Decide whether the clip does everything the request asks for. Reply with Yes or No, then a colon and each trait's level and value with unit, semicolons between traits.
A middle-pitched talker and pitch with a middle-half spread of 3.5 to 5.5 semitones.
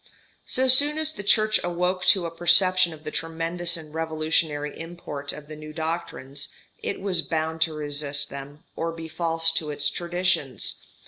No: medium, 165 Hz; narrow, 2.5 semitones